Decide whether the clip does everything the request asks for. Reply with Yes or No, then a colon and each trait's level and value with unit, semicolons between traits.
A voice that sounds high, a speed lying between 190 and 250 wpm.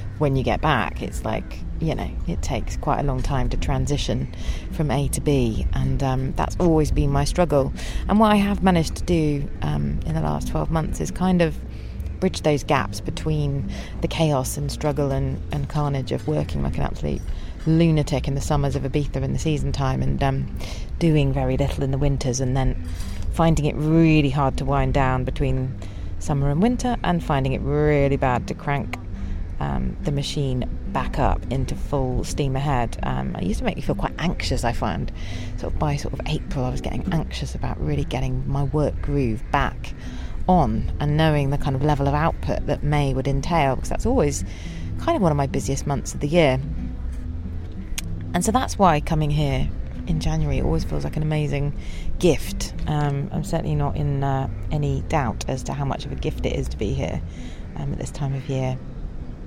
No: low, 135 Hz; average, 200 wpm